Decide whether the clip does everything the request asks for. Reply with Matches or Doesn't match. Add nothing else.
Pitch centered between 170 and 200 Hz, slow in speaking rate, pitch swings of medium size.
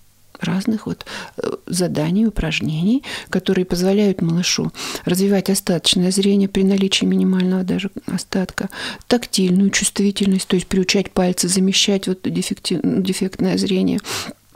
Doesn't match